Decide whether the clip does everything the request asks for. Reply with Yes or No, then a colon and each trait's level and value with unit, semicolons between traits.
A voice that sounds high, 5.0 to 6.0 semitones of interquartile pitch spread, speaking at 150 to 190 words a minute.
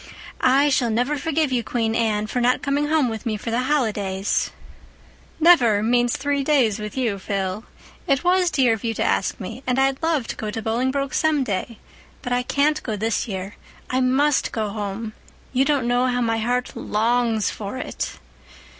No: high, 245 Hz; average, 3.9 semitones; average, 180 wpm